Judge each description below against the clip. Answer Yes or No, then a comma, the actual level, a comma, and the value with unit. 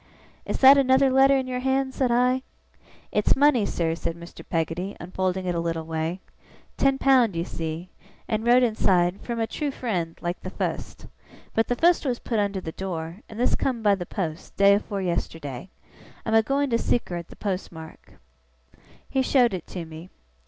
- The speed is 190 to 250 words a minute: Yes, average, 195 wpm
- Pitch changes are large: Yes, wide, 6.8 semitones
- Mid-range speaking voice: No, high, 200 Hz